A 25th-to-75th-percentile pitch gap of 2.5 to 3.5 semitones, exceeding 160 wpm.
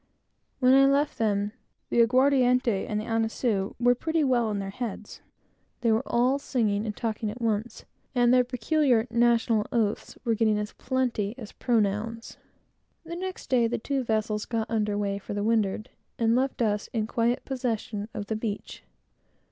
Yes: average, 2.9 semitones; average, 170 wpm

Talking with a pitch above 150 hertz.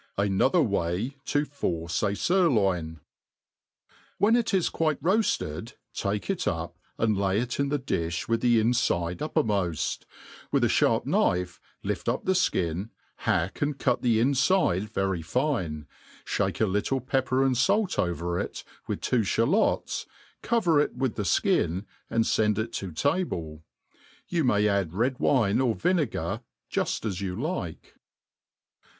No: low, 110 Hz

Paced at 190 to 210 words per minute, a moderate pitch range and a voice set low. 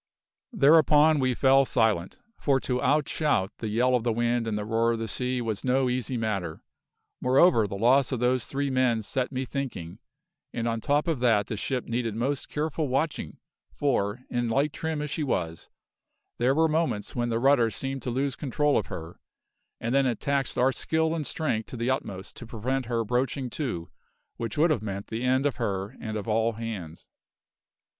Yes: average, 195 wpm; average, 3.6 semitones; low, 125 Hz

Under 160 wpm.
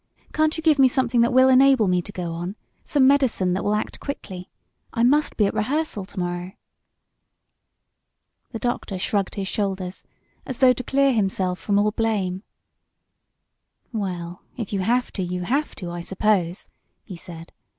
No: average, 170 wpm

